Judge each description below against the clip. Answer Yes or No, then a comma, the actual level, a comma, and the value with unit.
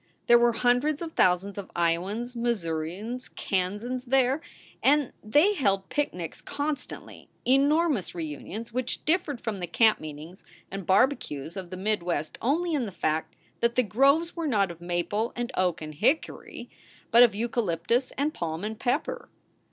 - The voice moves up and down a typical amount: No, wide, 6.5 semitones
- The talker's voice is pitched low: No, high, 225 Hz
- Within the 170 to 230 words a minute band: No, average, 160 wpm